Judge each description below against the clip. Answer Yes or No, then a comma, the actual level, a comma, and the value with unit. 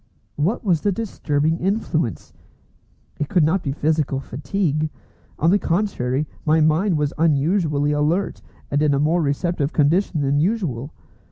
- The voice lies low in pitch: No, medium, 155 Hz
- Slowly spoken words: No, average, 145 wpm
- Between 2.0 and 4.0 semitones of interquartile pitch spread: Yes, average, 3.6 semitones